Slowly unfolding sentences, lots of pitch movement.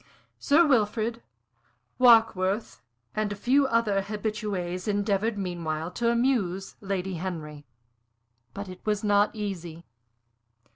No: slow, 105 wpm; average, 3.5 semitones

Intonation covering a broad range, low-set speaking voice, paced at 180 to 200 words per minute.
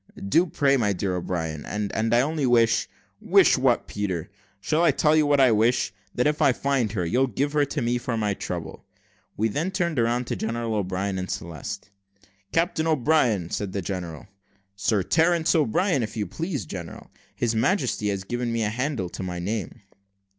Yes: wide, 6.4 semitones; low, 115 Hz; average, 190 wpm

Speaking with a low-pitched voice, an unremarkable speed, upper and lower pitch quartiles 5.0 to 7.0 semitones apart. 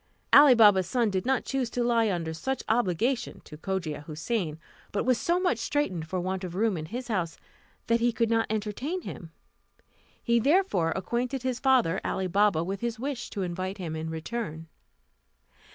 No: high, 215 Hz; average, 180 wpm; average, 5.3 semitones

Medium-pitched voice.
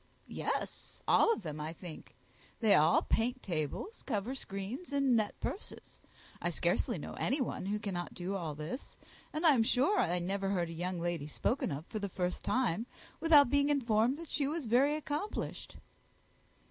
No: high, 215 Hz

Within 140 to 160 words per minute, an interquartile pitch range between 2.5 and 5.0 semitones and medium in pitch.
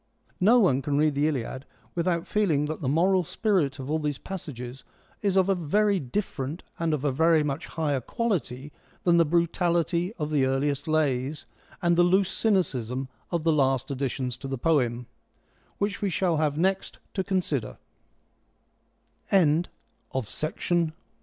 Yes: average, 145 wpm; average, 4.6 semitones; medium, 155 Hz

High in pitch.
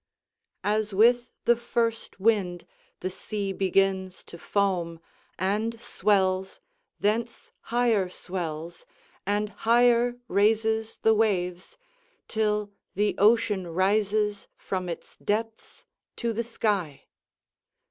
Yes: high, 205 Hz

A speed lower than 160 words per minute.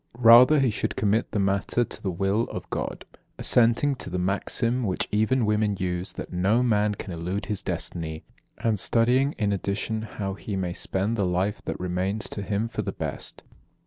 No: average, 185 wpm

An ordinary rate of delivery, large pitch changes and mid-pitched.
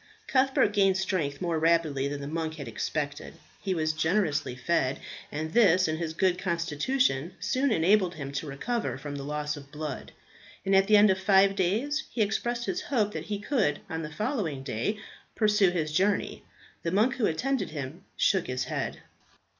Yes: average, 180 wpm; wide, 5.7 semitones; medium, 175 Hz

